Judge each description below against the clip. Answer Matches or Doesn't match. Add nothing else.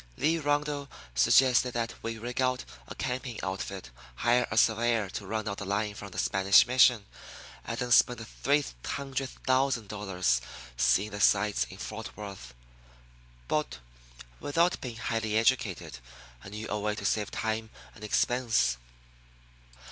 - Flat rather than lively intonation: Doesn't match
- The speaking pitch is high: Doesn't match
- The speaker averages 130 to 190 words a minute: Matches